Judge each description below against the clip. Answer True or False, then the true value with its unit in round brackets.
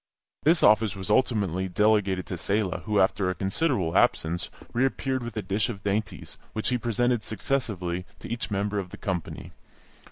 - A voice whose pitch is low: True (105 Hz)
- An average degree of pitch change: True (3.8 semitones)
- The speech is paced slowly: False (165 wpm)